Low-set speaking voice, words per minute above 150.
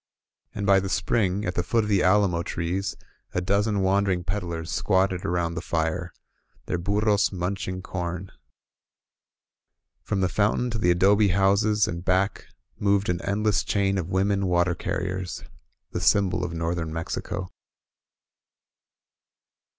No: very low, 95 Hz; average, 145 wpm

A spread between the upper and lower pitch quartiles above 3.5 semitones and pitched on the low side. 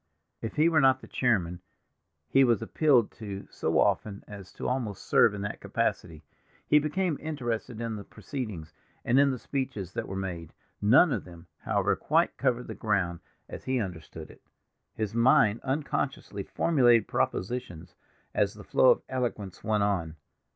Yes: average, 5.3 semitones; low, 110 Hz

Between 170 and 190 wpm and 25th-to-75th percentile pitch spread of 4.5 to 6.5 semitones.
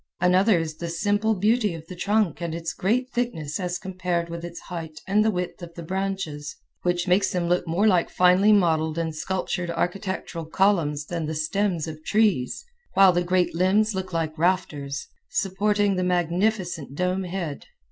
No: average, 175 wpm; average, 2.9 semitones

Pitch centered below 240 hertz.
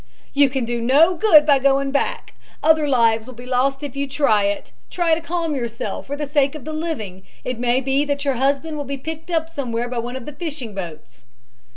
No: very high, 275 Hz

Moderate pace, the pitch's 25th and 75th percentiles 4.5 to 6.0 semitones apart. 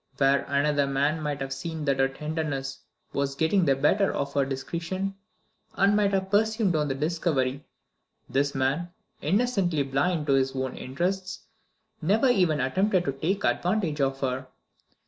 Yes: average, 155 wpm; wide, 5.4 semitones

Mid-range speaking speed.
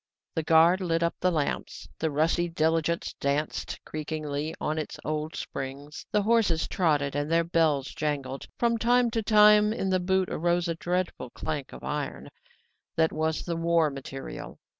Yes: average, 160 wpm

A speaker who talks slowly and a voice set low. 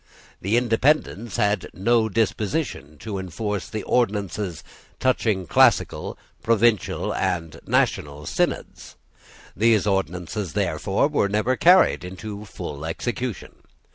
Yes: slow, 105 wpm; low, 105 Hz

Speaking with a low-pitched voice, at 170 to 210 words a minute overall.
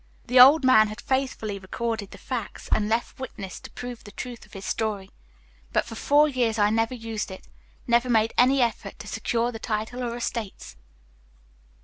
No: high, 230 Hz; average, 185 wpm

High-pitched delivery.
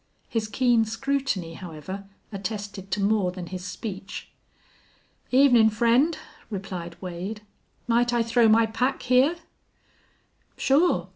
Yes: high, 220 Hz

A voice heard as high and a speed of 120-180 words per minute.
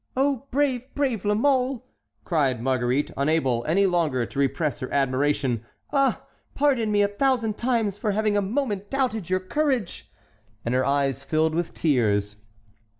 Yes: high, 195 Hz; average, 150 wpm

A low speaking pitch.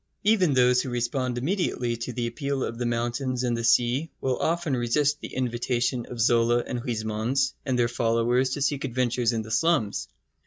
Yes: low, 125 Hz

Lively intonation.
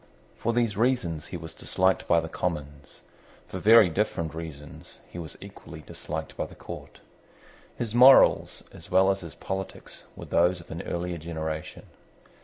No: average, 3.7 semitones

